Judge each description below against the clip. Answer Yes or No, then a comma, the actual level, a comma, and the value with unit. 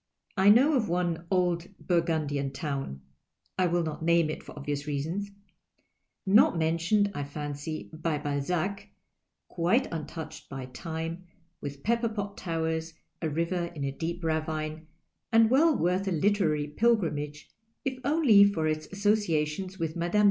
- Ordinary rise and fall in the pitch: Yes, average, 4.2 semitones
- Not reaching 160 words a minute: Yes, average, 150 wpm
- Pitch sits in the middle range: Yes, medium, 165 Hz